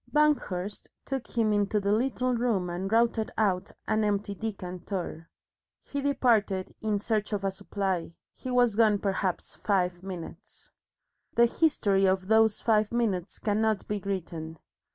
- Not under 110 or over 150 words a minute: Yes, average, 140 wpm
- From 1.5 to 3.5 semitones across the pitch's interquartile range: Yes, average, 2.9 semitones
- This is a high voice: Yes, high, 205 Hz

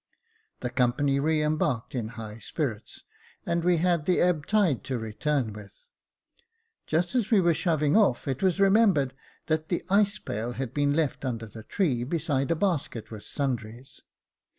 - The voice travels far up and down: Yes, wide, 6.1 semitones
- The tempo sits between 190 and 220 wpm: No, average, 165 wpm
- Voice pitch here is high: No, medium, 145 Hz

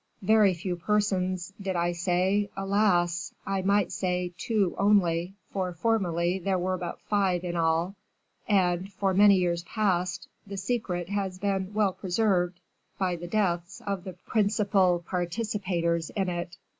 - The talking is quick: No, average, 145 wpm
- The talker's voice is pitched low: No, medium, 185 Hz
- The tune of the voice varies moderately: No, narrow, 2.2 semitones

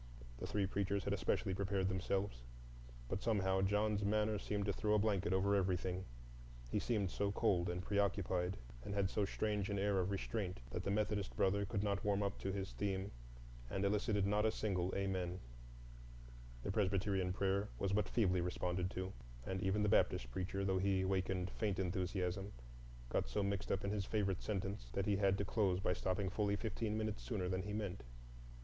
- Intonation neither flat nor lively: No, narrow, 1.6 semitones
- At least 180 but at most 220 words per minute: Yes, average, 185 wpm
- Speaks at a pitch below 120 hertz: Yes, low, 100 Hz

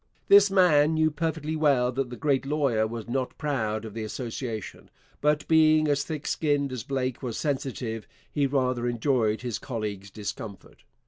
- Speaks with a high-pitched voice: No, low, 135 Hz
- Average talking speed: Yes, average, 165 wpm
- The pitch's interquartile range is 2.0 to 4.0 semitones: No, average, 4.5 semitones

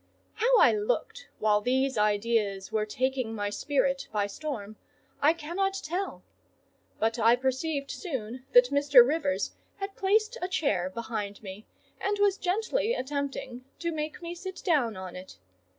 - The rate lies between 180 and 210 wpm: No, average, 150 wpm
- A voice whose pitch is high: Yes, very high, 270 Hz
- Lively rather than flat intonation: Yes, wide, 8.2 semitones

